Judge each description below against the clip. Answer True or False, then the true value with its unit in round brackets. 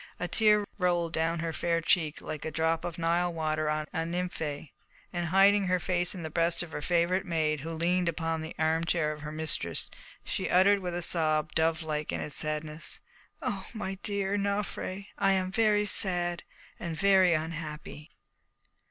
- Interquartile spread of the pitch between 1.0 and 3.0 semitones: True (2.7 semitones)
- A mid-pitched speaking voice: True (170 Hz)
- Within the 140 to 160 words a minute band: False (175 wpm)